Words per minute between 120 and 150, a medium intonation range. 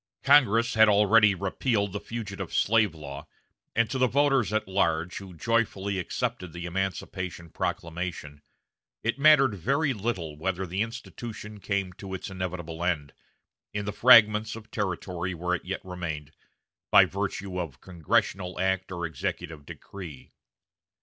Yes: average, 140 wpm; average, 4.0 semitones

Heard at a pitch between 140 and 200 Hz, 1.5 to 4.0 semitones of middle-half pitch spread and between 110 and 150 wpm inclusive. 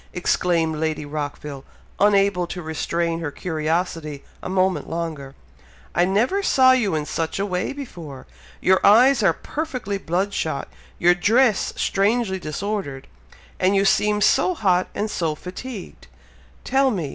No: medium, 185 Hz; average, 4.5 semitones; average, 140 wpm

